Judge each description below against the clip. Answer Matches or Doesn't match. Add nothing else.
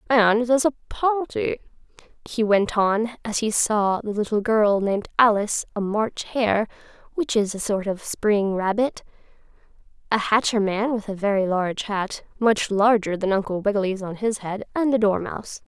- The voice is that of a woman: Matches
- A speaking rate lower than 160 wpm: Doesn't match